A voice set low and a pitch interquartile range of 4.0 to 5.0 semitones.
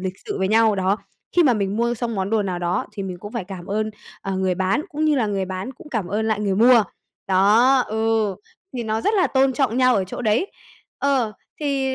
No: high, 220 Hz; average, 4.7 semitones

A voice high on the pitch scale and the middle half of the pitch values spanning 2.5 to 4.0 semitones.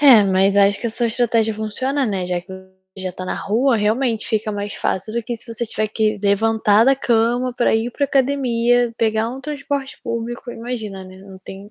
Yes: high, 225 Hz; average, 3.1 semitones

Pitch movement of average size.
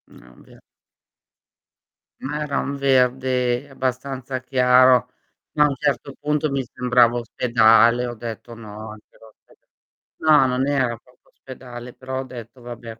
No: narrow, 1.9 semitones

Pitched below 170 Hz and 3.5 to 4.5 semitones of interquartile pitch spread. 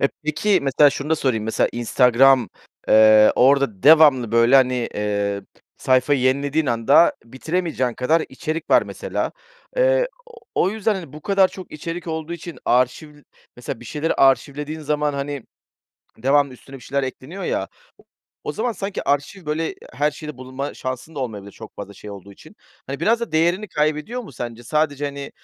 Yes: medium, 140 Hz; average, 4.1 semitones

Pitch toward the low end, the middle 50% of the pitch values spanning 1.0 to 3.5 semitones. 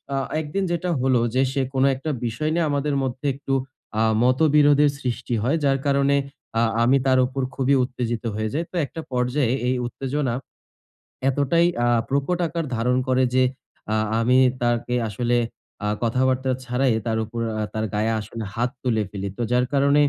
Yes: low, 130 Hz; average, 2.8 semitones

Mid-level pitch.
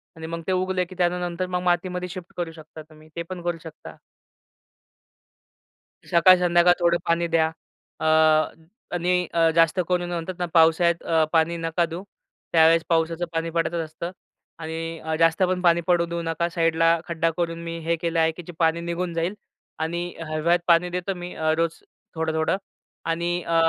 Yes: medium, 170 Hz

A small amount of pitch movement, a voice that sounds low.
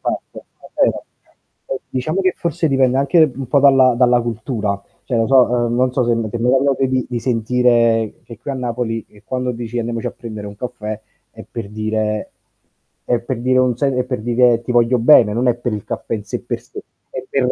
Yes: narrow, 2.2 semitones; low, 120 Hz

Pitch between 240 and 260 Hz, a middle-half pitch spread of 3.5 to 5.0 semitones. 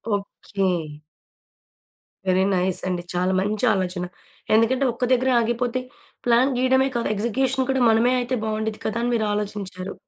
No: high, 220 Hz; average, 4.3 semitones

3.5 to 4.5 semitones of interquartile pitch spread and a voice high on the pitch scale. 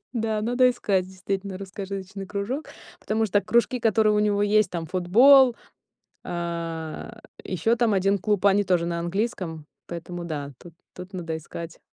Yes: average, 3.8 semitones; high, 195 Hz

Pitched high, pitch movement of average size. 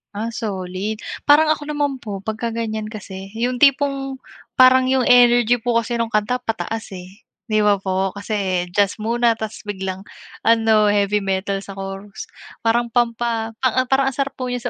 Yes: high, 225 Hz; average, 3.5 semitones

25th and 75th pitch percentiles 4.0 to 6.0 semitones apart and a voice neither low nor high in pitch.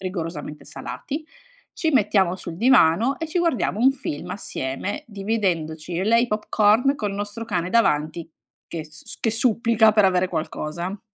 No: wide, 5.4 semitones; high, 205 Hz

